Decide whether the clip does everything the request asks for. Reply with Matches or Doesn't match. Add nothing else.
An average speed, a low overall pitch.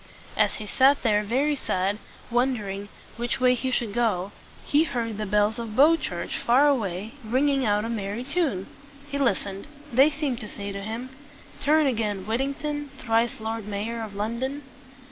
Doesn't match